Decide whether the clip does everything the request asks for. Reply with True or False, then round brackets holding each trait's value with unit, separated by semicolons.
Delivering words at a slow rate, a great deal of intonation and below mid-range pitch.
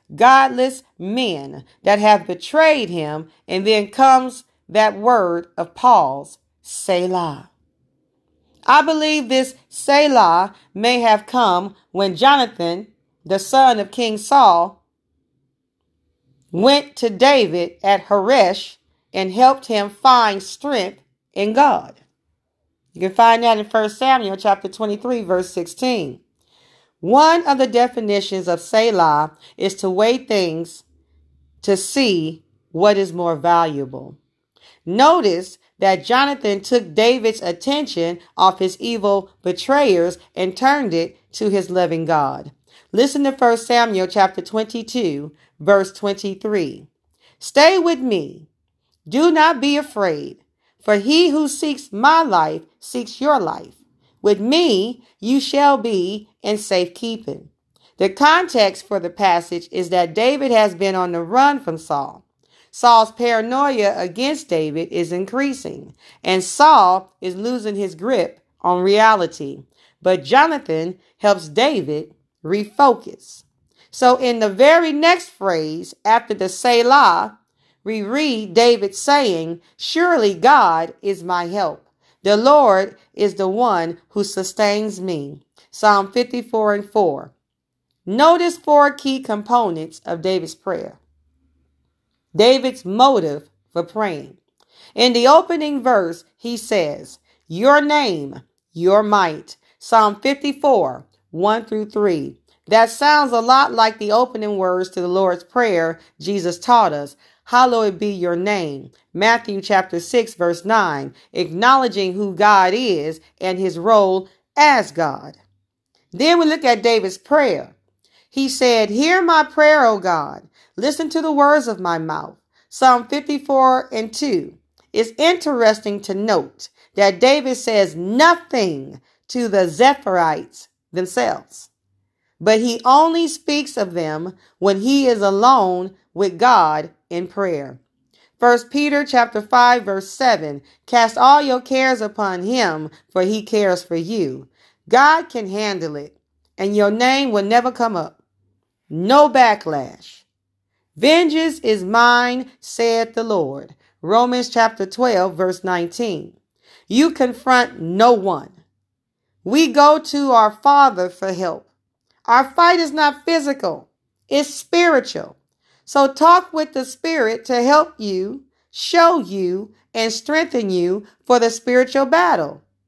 False (125 wpm; 6.2 semitones; 215 Hz)